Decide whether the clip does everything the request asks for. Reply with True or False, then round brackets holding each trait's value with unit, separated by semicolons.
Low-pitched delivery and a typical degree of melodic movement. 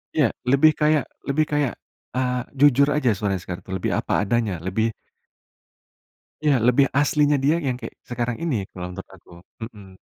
False (125 Hz; 6.1 semitones)